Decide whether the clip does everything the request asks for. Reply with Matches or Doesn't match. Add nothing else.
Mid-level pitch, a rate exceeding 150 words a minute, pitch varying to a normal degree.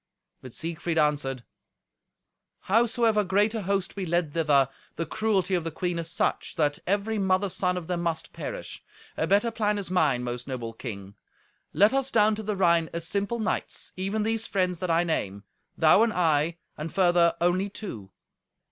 Matches